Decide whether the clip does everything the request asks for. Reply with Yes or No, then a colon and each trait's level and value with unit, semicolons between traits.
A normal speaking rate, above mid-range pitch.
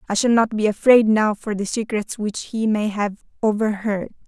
Yes: average, 195 wpm; high, 215 Hz